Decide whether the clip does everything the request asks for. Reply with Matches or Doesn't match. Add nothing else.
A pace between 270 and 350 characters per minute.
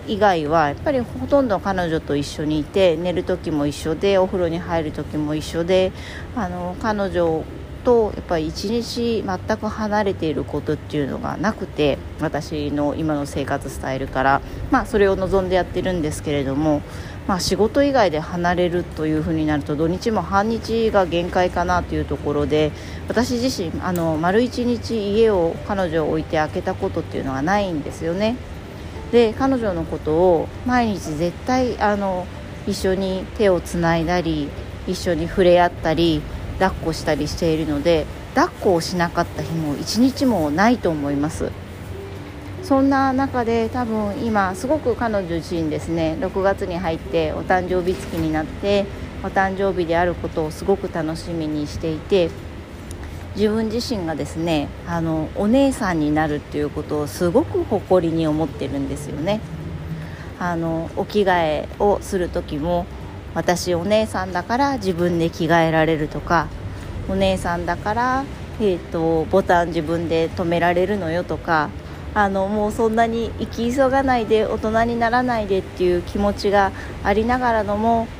Matches